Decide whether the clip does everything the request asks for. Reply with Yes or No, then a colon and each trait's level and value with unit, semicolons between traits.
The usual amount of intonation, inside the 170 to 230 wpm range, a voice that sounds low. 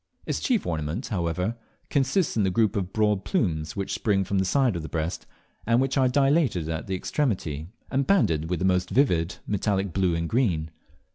No: wide, 7.0 semitones; average, 195 wpm; very low, 95 Hz